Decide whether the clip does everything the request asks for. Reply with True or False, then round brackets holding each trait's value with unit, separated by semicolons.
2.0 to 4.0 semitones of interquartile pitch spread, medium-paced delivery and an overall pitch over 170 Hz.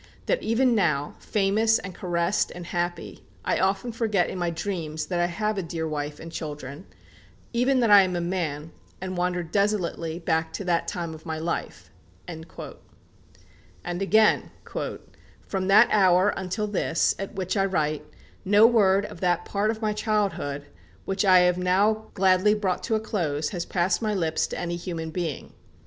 True (3.5 semitones; 170 wpm; 185 Hz)